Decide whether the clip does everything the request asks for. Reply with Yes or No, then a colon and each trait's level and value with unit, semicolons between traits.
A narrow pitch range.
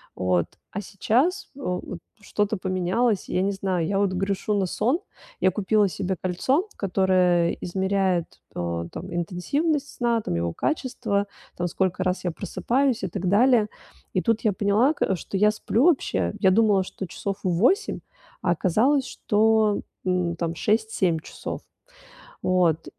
No: average, 3.5 semitones